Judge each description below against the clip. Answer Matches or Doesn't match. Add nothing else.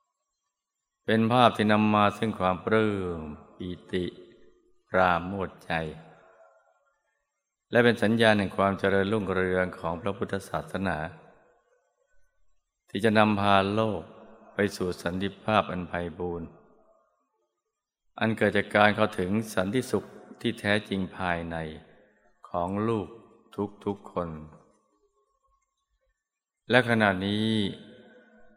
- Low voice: Matches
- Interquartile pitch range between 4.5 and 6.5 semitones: Doesn't match